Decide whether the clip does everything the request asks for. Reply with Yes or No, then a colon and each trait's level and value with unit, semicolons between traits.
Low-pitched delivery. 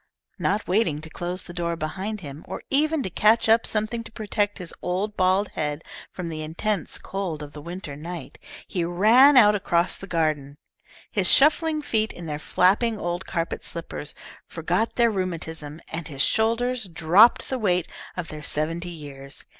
No: medium, 180 Hz